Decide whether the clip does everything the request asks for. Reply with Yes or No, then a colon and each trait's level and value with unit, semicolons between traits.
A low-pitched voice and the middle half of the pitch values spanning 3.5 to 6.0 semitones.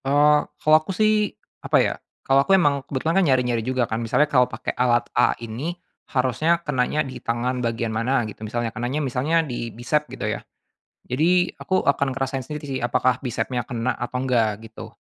Yes: low, 130 Hz; average, 3.9 semitones